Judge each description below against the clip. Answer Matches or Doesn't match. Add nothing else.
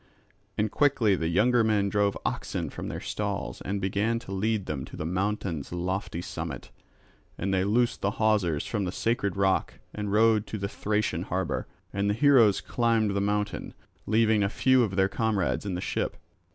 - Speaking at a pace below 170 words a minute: Doesn't match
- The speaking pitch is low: Matches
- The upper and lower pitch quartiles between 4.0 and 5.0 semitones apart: Doesn't match